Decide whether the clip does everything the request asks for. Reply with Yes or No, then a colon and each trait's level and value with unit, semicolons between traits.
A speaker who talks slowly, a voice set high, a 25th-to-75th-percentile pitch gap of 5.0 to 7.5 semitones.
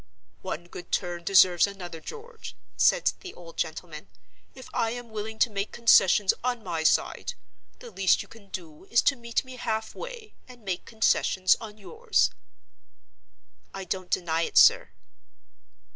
No: average, 155 wpm; high, 205 Hz; wide, 5.5 semitones